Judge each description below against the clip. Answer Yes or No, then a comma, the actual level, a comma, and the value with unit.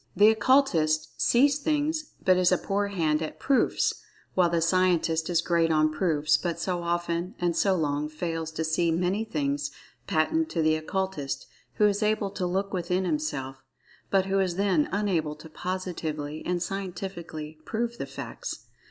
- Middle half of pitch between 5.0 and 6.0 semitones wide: No, average, 3.8 semitones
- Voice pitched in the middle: Yes, medium, 175 Hz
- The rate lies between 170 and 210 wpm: No, average, 160 wpm